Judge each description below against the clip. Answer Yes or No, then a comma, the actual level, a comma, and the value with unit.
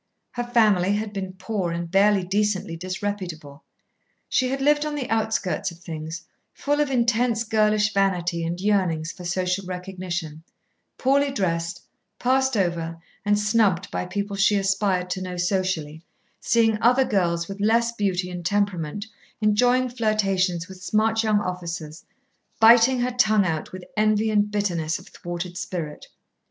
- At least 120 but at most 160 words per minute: Yes, average, 145 wpm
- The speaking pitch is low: No, high, 195 Hz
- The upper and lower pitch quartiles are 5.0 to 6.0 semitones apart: No, average, 3.7 semitones